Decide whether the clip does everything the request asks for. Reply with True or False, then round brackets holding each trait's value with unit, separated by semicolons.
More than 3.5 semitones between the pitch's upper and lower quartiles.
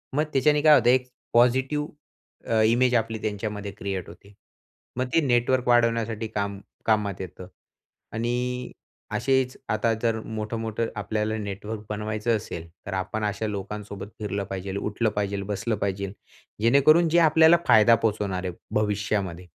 False (3.1 semitones)